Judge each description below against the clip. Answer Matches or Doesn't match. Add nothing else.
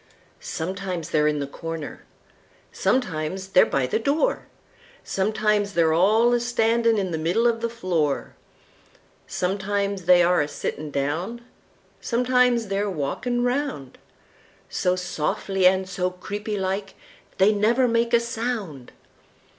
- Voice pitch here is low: Doesn't match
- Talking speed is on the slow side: Matches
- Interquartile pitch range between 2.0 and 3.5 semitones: Doesn't match